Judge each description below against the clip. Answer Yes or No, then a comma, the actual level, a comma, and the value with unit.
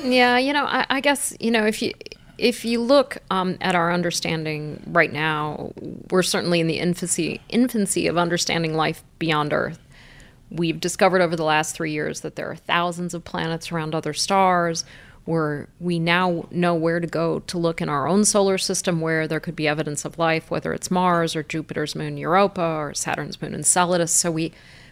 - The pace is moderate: Yes, average, 195 wpm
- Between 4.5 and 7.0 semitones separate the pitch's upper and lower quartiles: No, average, 2.8 semitones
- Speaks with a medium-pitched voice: Yes, medium, 170 Hz